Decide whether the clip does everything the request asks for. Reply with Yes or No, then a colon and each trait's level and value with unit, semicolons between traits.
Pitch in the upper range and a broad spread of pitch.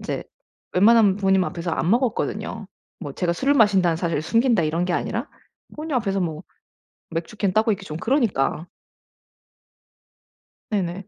No: high, 195 Hz; average, 4.6 semitones